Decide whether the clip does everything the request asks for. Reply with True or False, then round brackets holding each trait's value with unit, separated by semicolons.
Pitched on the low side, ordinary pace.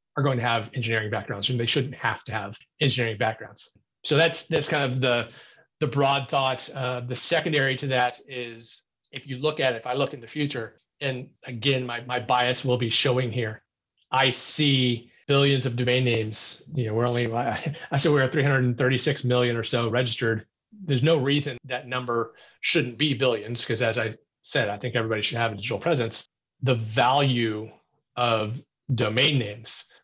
True (125 Hz; 190 wpm)